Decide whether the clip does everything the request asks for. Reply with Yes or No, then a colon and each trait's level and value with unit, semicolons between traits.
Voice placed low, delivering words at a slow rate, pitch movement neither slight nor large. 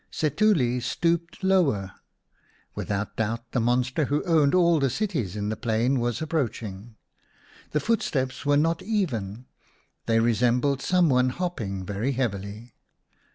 No: low, 125 Hz; slow, 130 wpm; wide, 6.1 semitones